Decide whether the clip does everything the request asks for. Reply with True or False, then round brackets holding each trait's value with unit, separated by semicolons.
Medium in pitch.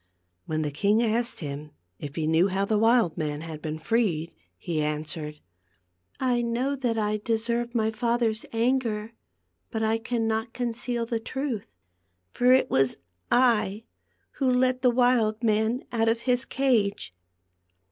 False (225 Hz)